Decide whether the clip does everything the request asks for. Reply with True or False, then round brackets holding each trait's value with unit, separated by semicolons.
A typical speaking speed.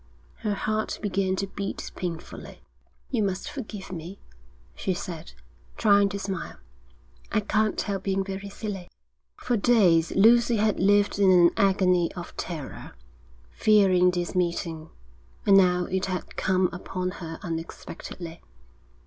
False (130 wpm)